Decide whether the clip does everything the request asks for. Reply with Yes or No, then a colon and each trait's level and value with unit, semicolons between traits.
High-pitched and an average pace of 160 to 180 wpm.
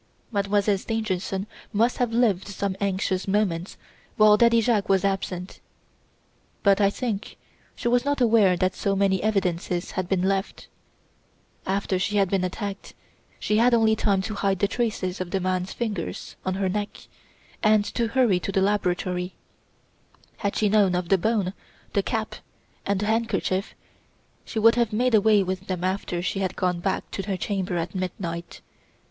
Yes: high, 195 Hz; average, 165 wpm